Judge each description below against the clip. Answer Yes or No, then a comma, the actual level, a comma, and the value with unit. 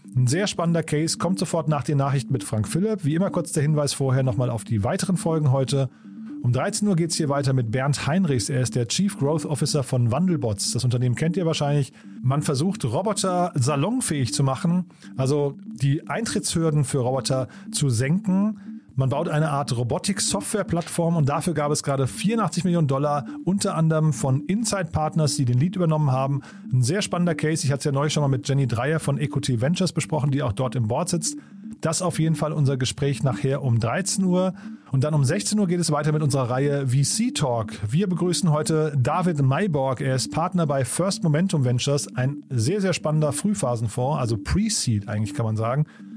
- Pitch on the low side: No, medium, 150 Hz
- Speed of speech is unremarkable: No, fast, 200 wpm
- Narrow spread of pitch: No, average, 4.8 semitones